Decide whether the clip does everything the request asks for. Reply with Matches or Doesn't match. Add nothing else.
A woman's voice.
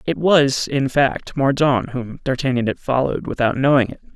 Doesn't match